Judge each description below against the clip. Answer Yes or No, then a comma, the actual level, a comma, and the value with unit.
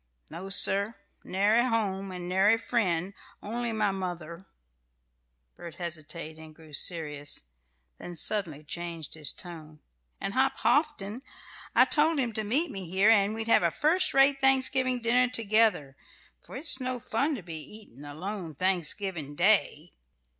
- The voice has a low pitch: No, high, 195 Hz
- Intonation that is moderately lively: No, wide, 5.7 semitones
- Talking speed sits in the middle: Yes, average, 145 wpm